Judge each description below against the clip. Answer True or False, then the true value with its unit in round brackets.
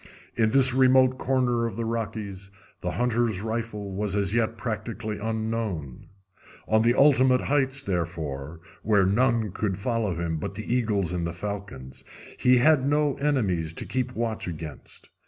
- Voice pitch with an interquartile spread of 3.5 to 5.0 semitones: True (4.6 semitones)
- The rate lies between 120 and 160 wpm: True (155 wpm)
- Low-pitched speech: True (110 Hz)